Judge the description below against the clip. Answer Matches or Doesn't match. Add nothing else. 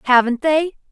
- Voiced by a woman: Matches